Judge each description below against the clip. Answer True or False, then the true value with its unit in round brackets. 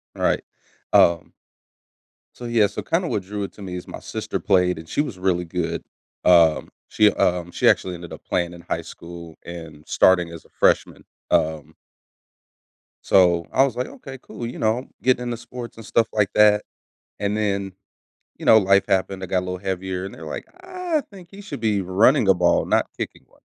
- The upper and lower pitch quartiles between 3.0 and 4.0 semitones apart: False (4.5 semitones)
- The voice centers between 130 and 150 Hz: False (95 Hz)